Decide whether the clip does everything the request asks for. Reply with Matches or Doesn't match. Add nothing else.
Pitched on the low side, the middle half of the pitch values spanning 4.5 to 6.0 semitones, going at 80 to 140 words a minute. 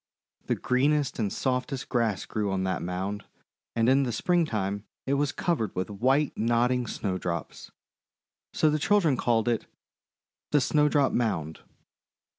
Matches